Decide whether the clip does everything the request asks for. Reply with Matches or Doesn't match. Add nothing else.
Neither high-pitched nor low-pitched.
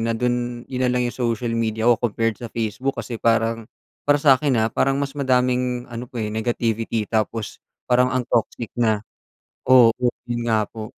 Doesn't match